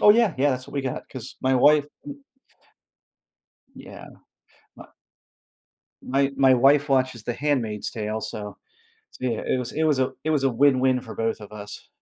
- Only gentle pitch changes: No, average, 3.6 semitones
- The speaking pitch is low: Yes, low, 130 Hz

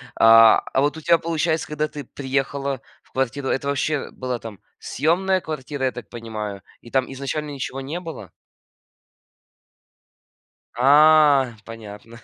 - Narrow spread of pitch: No, average, 4.1 semitones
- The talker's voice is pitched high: No, low, 135 Hz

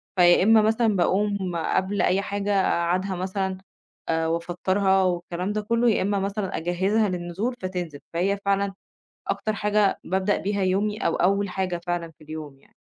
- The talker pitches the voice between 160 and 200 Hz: Yes, high, 190 Hz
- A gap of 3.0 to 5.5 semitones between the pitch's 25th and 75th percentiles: No, narrow, 2.5 semitones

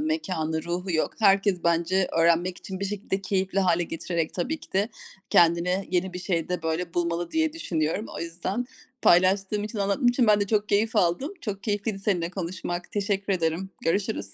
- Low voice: No, high, 190 Hz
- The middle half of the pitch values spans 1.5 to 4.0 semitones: Yes, average, 3.1 semitones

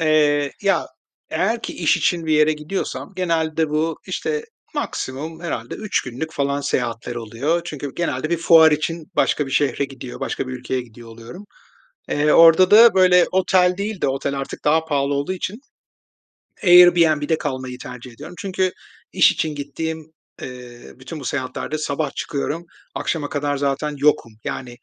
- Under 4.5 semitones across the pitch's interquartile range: Yes, average, 3.7 semitones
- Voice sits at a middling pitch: Yes, medium, 150 Hz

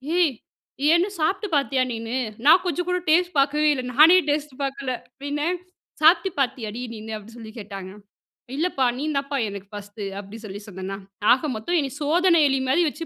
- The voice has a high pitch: Yes, very high, 275 Hz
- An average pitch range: No, wide, 6.6 semitones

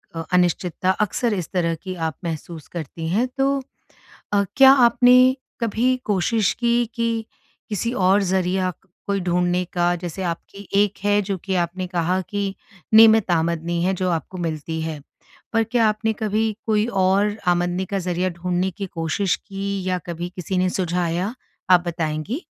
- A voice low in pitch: No, medium, 185 Hz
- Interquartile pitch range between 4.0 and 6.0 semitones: No, average, 3.4 semitones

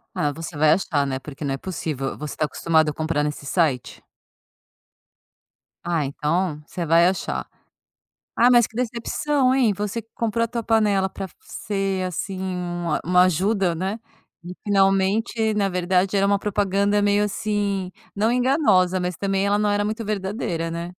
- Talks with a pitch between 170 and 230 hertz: Yes, high, 190 Hz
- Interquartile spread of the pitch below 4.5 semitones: Yes, average, 3.7 semitones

